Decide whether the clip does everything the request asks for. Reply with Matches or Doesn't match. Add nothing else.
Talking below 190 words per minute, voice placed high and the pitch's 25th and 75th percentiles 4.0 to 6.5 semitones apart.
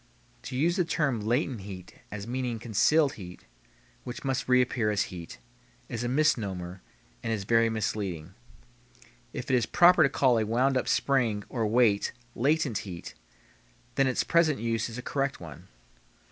Doesn't match